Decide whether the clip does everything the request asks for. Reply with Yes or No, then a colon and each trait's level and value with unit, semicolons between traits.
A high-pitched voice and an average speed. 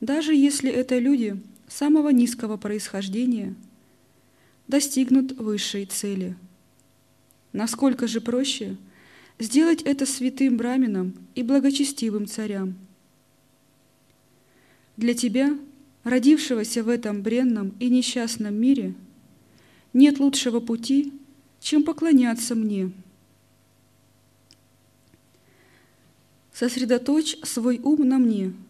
No: high, 230 Hz; slow, 85 wpm